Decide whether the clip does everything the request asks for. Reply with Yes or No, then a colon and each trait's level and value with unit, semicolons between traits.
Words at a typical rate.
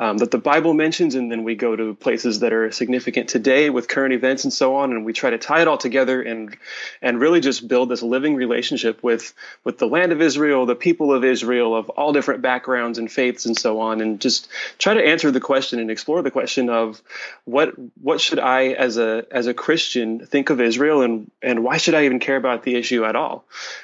No: fast, 230 wpm